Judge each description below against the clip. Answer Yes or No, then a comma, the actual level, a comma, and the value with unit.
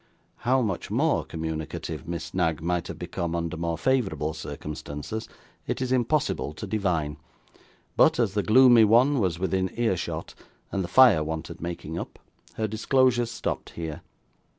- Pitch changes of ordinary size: No, wide, 6.4 semitones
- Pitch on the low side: Yes, very low, 95 Hz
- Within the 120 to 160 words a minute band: Yes, average, 150 wpm